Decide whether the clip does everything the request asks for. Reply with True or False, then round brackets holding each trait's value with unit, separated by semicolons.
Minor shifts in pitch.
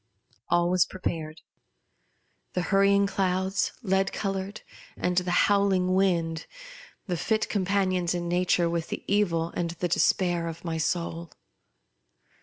True (2.3 semitones)